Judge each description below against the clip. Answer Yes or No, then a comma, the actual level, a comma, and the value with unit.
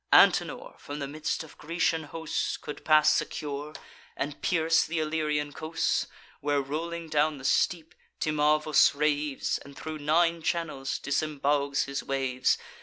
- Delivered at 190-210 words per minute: No, slow, 135 wpm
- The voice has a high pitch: No, medium, 150 Hz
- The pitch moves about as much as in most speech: No, narrow, 1.9 semitones